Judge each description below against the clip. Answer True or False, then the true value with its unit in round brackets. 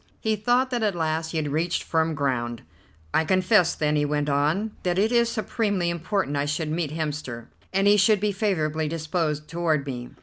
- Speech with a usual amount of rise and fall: True (4.9 semitones)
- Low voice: False (165 Hz)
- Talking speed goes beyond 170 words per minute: True (195 wpm)